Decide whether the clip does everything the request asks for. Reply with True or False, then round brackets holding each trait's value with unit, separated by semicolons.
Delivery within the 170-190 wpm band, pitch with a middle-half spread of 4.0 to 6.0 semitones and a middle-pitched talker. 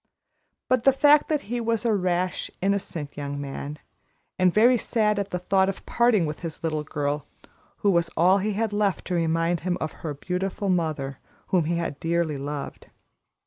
True (185 wpm; 4.7 semitones; 180 Hz)